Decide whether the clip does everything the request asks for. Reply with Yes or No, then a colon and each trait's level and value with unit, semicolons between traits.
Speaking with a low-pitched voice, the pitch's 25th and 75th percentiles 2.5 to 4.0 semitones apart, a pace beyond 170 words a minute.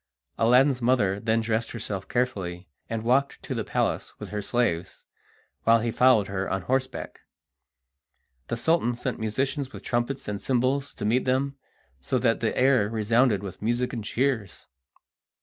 No: low, 120 Hz; average, 3.4 semitones; average, 155 wpm